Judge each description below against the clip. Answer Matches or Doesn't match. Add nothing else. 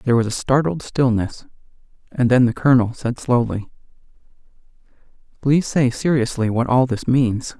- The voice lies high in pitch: Doesn't match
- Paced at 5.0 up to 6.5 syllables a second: Matches